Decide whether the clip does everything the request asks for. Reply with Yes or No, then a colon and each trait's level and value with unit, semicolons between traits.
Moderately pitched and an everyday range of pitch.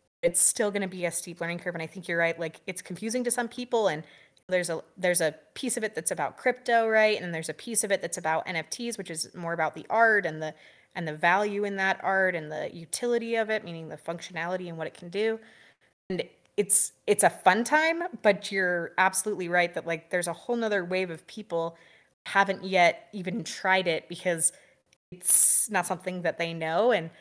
Yes: medium, 180 Hz; average, 4.0 semitones